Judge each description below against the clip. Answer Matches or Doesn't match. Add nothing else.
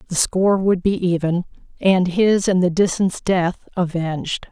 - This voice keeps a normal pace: Matches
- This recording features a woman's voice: Matches